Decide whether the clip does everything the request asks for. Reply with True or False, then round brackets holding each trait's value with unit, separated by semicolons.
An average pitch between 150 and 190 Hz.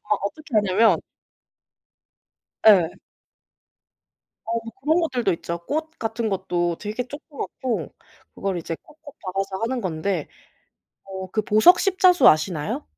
False (210 Hz)